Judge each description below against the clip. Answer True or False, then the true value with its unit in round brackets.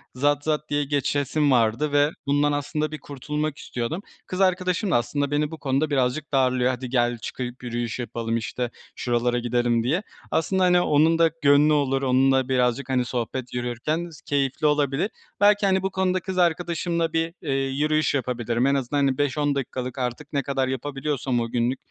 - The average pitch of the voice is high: False (140 Hz)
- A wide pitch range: False (3.6 semitones)